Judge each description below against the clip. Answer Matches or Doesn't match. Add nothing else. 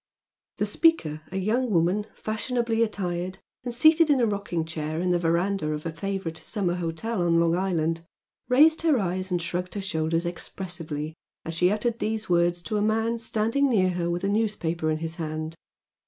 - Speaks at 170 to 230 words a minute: Matches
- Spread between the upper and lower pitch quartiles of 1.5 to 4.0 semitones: Doesn't match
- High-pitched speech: Doesn't match